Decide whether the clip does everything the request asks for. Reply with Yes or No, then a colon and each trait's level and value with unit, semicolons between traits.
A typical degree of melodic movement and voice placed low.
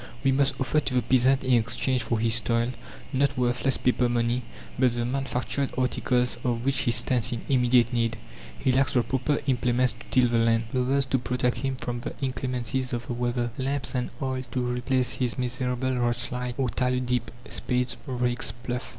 No: narrow, 1.4 semitones; low, 125 Hz